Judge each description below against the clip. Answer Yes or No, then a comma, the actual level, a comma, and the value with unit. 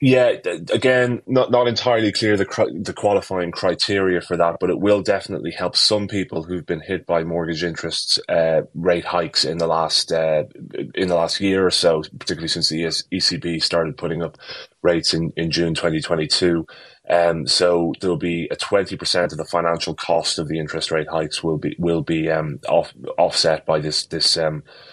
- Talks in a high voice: No, very low, 85 Hz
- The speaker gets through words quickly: No, average, 185 wpm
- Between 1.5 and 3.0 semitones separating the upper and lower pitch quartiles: Yes, average, 2.7 semitones